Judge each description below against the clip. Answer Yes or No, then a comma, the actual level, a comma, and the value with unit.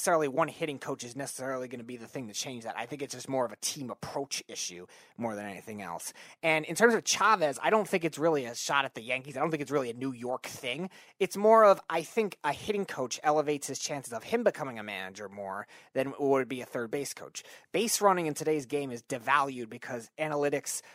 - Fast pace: Yes, fast, 245 wpm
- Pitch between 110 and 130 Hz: No, medium, 140 Hz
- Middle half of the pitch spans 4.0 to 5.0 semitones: Yes, average, 4.6 semitones